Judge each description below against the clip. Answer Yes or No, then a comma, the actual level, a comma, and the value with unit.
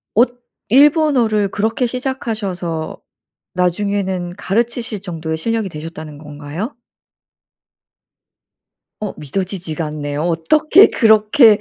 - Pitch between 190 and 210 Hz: Yes, high, 200 Hz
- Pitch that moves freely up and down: Yes, wide, 6.0 semitones